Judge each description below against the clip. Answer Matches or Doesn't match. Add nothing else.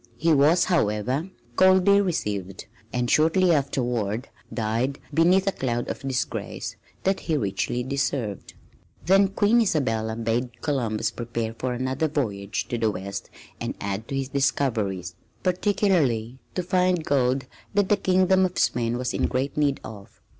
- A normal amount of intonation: Doesn't match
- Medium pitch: Doesn't match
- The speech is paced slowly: Doesn't match